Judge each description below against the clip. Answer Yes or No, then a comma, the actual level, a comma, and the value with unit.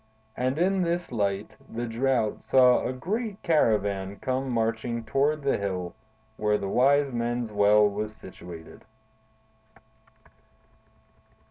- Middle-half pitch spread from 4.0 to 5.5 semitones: Yes, average, 4.8 semitones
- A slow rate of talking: Yes, slow, 115 wpm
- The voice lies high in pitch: No, low, 115 Hz